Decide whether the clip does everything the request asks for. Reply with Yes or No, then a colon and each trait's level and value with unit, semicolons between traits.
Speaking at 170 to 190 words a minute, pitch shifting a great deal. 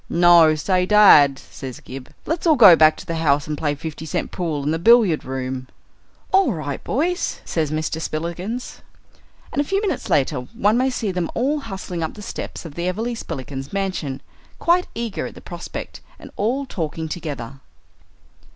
Yes: average, 180 wpm; wide, 7.3 semitones